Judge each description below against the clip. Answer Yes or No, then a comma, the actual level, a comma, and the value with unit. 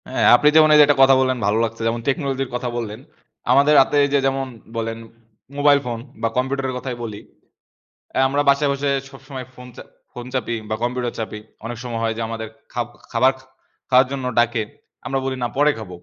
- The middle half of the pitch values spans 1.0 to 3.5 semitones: Yes, average, 2.8 semitones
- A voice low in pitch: Yes, low, 125 Hz